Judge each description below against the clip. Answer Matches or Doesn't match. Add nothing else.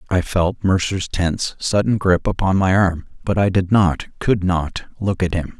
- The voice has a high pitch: Doesn't match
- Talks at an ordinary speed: Matches